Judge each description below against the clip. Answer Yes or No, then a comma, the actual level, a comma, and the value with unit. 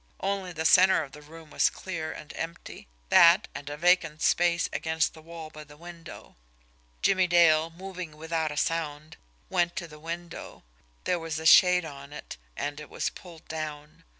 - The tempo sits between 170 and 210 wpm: Yes, average, 175 wpm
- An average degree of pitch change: No, narrow, 2.2 semitones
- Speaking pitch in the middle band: Yes, medium, 165 Hz